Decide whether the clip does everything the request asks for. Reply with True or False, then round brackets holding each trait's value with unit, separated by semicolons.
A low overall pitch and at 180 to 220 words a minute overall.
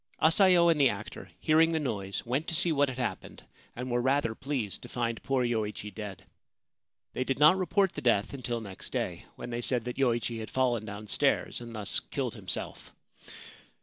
True (125 Hz; 190 wpm)